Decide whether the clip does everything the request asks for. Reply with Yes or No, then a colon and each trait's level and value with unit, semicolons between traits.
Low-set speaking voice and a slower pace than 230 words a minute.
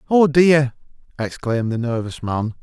Yes: low, 130 Hz; slow, 135 wpm